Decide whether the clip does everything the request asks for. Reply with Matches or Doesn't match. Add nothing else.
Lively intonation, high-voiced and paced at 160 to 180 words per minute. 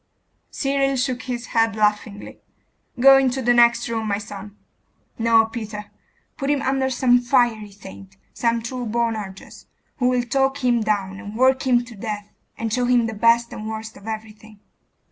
Doesn't match